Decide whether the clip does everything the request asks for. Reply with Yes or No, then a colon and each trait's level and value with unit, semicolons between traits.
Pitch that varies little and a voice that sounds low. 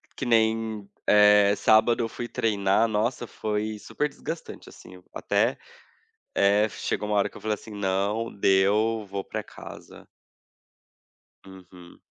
Yes: narrow, 2.1 semitones; low, 105 Hz